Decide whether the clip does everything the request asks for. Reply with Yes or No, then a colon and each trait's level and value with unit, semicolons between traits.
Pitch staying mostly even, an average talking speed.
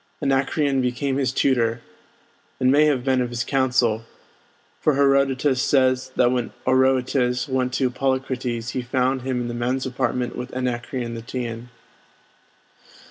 Yes: narrow, 1.4 semitones; average, 145 wpm